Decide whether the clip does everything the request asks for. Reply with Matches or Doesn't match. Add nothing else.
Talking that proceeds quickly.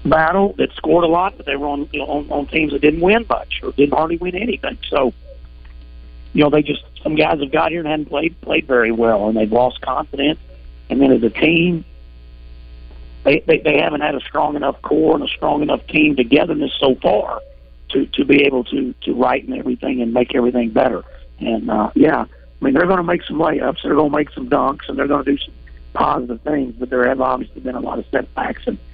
Matches